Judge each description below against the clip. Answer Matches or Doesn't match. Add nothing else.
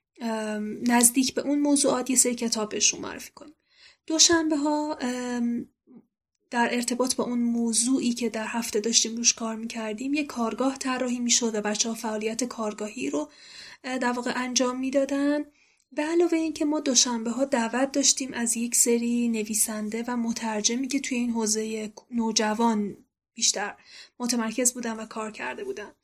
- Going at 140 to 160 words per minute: Matches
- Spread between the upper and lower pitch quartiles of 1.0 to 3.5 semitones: Matches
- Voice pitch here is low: Doesn't match